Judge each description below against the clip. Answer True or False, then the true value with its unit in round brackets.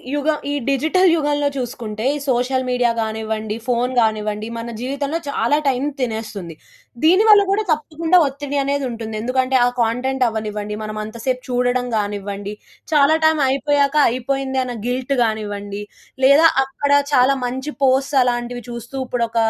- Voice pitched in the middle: False (250 Hz)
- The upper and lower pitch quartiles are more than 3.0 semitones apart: True (4.1 semitones)